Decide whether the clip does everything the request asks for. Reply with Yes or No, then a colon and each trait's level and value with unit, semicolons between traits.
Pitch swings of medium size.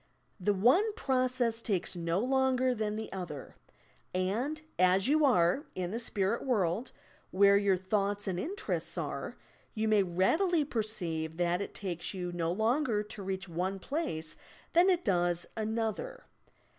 No: wide, 5.8 semitones